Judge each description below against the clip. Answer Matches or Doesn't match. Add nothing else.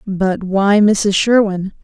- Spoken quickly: Doesn't match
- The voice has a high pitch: Matches